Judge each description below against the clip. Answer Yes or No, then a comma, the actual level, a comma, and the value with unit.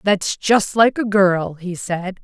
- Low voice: No, high, 190 Hz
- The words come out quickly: No, average, 190 wpm